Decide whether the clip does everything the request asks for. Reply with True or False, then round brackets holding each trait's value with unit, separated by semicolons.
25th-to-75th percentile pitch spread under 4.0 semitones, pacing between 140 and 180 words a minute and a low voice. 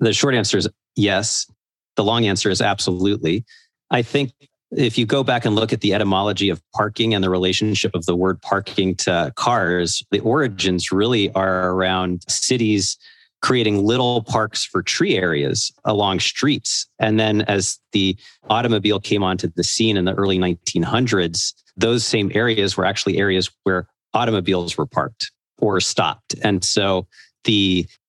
True (3.1 semitones; 160 wpm; 100 Hz)